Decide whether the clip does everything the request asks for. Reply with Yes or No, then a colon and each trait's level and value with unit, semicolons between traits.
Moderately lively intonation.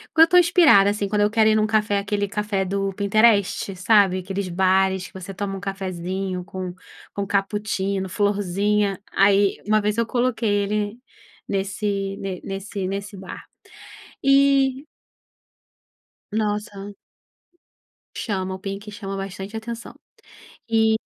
No: narrow, 1.7 semitones